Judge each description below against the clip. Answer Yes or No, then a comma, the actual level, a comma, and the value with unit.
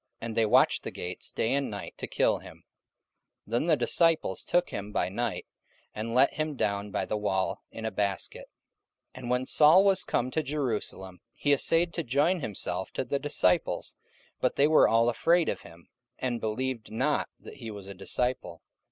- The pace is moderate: Yes, average, 190 wpm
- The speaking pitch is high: No, low, 120 Hz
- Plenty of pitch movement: Yes, wide, 5.9 semitones